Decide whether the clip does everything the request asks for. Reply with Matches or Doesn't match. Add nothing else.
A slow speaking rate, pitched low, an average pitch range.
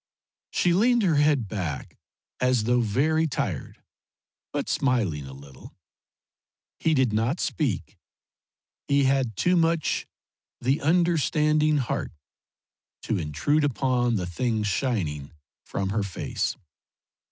Doesn't match